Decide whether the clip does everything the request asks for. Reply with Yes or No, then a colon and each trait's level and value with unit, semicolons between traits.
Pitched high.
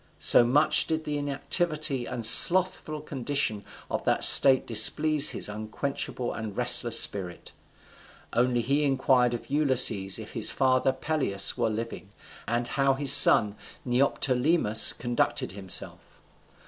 No: low, 130 Hz